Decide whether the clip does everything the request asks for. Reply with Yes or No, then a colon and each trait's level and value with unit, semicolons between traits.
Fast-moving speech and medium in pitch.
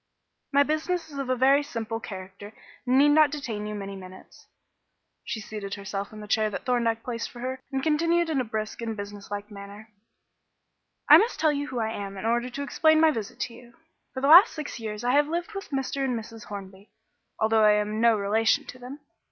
No: fast, 215 wpm; high, 230 Hz